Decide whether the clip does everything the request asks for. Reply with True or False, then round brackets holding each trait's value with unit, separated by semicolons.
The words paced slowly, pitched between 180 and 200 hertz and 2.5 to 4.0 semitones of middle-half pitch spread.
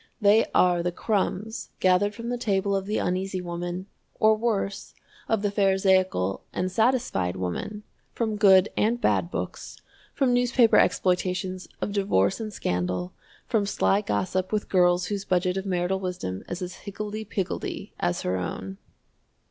False (150 wpm; 190 Hz; 2.8 semitones)